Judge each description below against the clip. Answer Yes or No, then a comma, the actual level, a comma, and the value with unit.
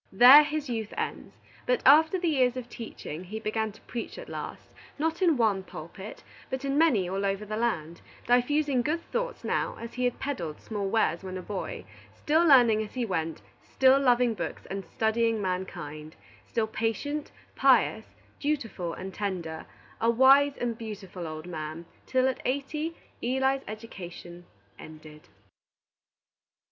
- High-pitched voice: Yes, high, 225 Hz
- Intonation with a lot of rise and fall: Yes, wide, 6.2 semitones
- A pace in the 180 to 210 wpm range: No, average, 155 wpm